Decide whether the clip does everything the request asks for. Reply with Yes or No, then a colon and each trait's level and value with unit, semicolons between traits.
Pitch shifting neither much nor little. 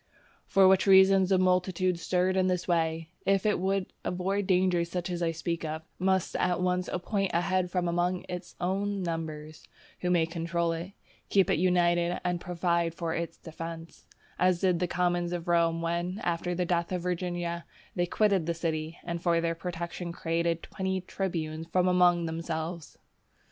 No: narrow, 1.6 semitones